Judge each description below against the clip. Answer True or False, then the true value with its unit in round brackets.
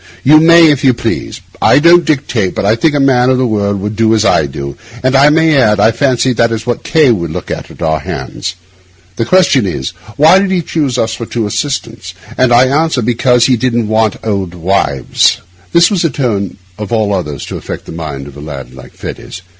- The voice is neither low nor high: False (115 Hz)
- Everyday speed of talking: False (225 wpm)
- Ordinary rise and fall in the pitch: False (6.0 semitones)